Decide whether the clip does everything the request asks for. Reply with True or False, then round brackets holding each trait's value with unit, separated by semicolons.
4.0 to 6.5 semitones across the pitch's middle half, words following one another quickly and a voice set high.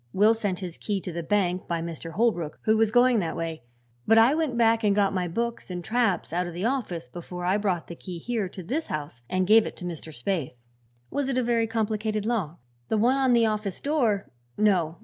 True (4.6 semitones; 225 wpm; 205 Hz)